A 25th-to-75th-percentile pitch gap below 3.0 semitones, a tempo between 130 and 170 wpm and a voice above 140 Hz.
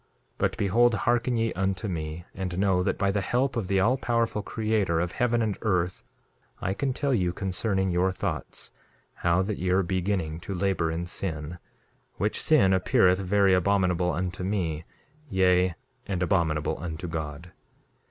No: narrow, 2.6 semitones; average, 165 wpm; very low, 95 Hz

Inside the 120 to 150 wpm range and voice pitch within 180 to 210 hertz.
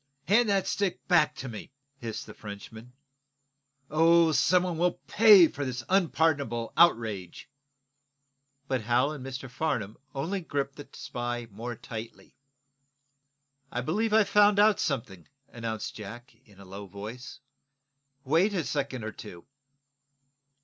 No: slow, 135 wpm; low, 135 Hz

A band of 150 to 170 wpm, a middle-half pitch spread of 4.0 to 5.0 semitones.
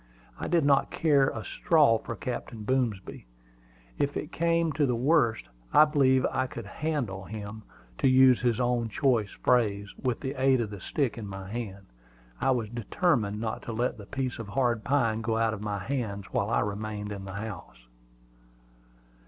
No: average, 180 wpm; average, 4.3 semitones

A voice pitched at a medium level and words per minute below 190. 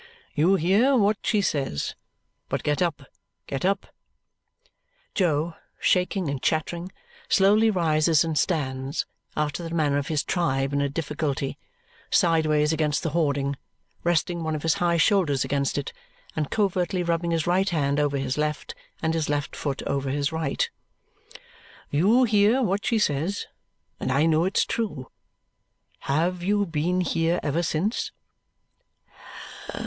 Yes: medium, 160 Hz; average, 145 wpm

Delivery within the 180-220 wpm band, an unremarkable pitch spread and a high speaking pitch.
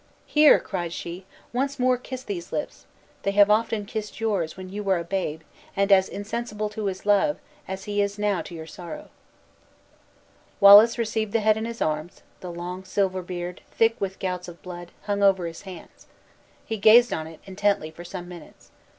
Yes: average, 185 wpm; average, 3.4 semitones; high, 200 Hz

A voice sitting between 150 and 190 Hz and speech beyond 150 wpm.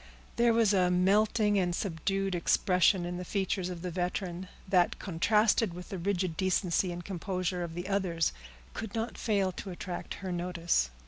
Yes: medium, 185 Hz; average, 170 wpm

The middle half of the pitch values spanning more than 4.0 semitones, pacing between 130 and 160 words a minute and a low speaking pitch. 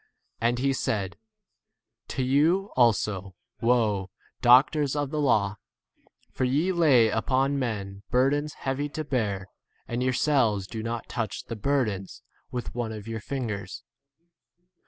Yes: average, 4.4 semitones; slow, 135 wpm; low, 120 Hz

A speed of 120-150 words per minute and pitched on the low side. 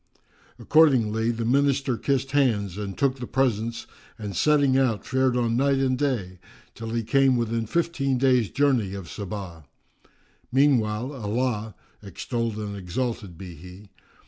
Yes: average, 140 wpm; low, 115 Hz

